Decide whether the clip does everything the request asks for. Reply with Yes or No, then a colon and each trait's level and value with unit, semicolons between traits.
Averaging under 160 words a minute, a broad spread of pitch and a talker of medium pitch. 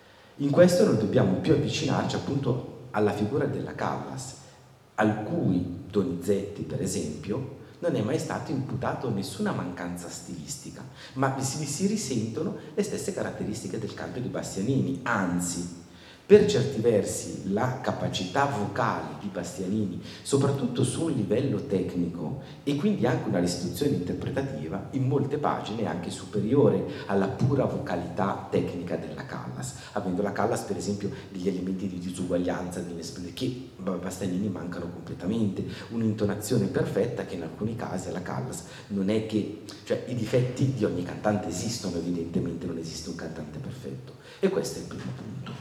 No: average, 145 wpm; wide, 6.2 semitones; low, 100 Hz